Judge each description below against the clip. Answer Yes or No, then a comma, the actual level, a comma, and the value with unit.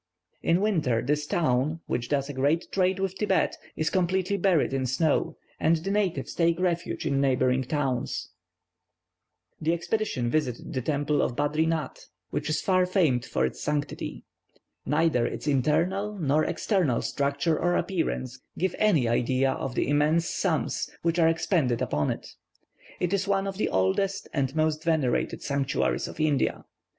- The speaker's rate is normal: Yes, average, 155 wpm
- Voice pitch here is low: No, medium, 155 Hz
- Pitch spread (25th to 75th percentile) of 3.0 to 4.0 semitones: No, average, 4.7 semitones